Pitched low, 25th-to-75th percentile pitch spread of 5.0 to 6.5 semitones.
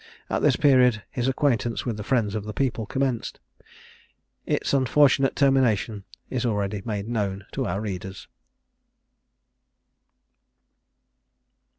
No: low, 115 Hz; average, 4.2 semitones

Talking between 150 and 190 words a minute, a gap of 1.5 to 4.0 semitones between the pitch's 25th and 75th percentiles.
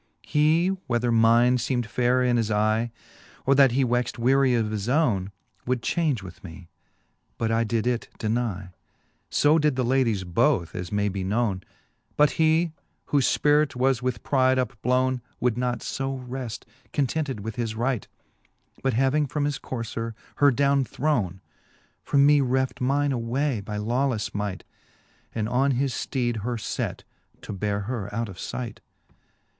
Yes: average, 160 wpm; average, 3.5 semitones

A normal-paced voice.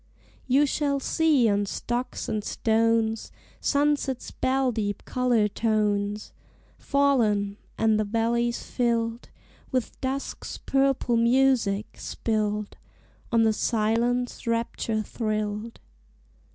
No: slow, 100 wpm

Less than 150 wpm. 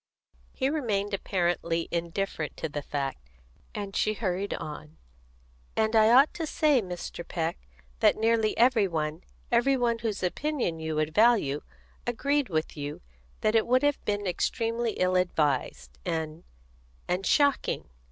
Yes: average, 140 wpm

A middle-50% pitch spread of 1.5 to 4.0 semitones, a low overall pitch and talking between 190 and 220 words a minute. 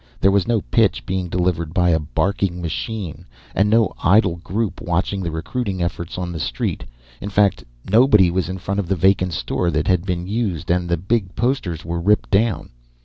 Yes: average, 2.8 semitones; very low, 95 Hz; average, 195 wpm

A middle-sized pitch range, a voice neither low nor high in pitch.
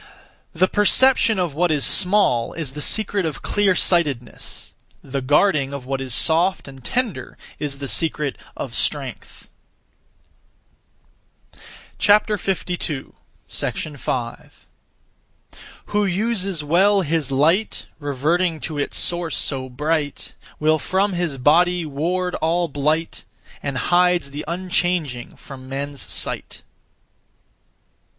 Yes: average, 4.5 semitones; medium, 160 Hz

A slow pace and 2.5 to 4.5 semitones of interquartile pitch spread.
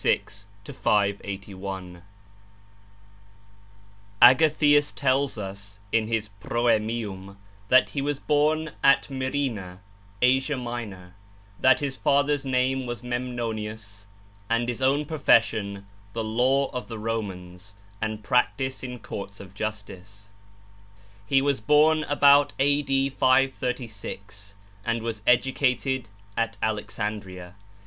No: slow, 105 wpm; average, 4.9 semitones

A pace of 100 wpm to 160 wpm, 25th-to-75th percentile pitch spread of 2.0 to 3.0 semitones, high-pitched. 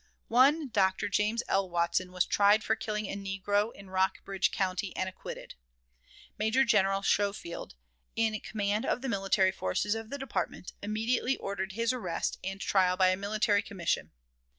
Yes: average, 155 wpm; narrow, 2.6 semitones; high, 200 Hz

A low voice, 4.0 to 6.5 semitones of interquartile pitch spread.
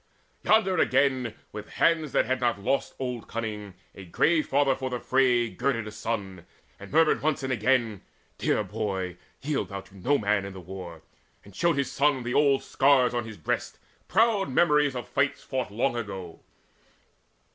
Yes: low, 125 Hz; average, 5.3 semitones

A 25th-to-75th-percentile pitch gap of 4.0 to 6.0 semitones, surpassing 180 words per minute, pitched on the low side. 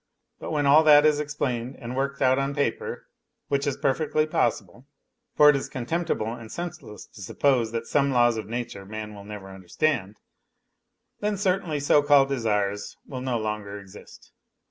No: average, 5.1 semitones; average, 165 wpm; low, 130 Hz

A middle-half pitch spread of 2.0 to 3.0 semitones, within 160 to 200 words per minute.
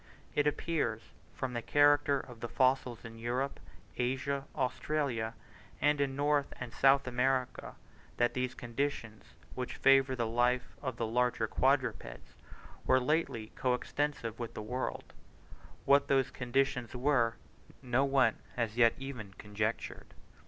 No: average, 2.7 semitones; slow, 135 wpm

